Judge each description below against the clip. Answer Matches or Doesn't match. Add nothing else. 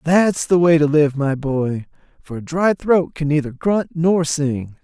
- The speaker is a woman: Doesn't match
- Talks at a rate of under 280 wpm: Matches